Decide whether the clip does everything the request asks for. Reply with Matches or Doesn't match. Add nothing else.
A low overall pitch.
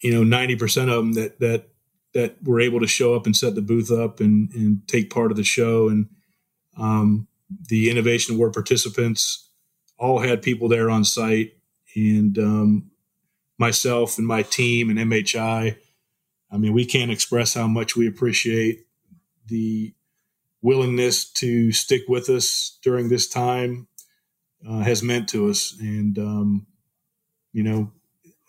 Matches